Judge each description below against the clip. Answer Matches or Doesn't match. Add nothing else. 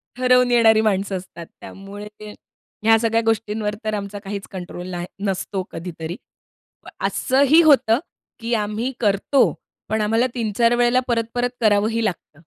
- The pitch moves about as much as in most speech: Matches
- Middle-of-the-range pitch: Doesn't match